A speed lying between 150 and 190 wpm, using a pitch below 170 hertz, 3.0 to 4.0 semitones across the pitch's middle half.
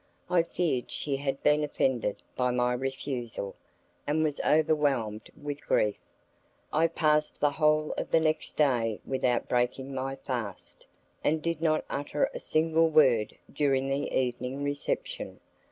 No: average, 140 wpm; medium, 140 Hz; average, 3.4 semitones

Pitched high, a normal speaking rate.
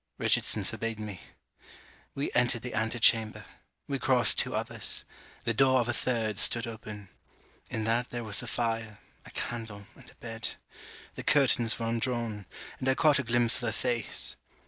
No: low, 115 Hz; average, 170 wpm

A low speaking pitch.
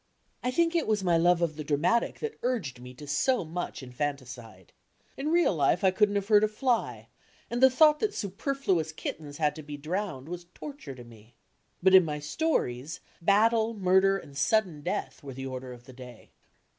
No: medium, 175 Hz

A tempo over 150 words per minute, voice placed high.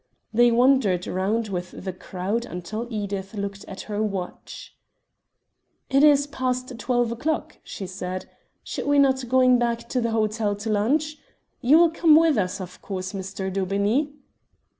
Yes: average, 160 wpm; high, 220 Hz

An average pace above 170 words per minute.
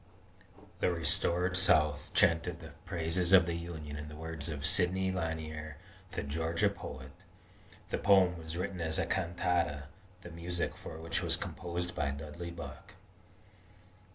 No: average, 145 wpm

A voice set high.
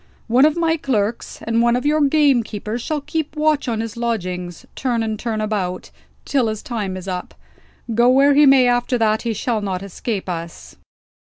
Yes: high, 235 Hz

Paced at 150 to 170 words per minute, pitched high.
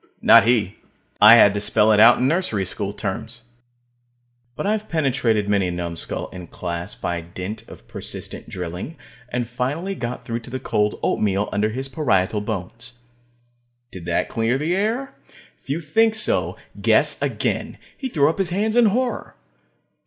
No: average, 165 wpm; low, 115 Hz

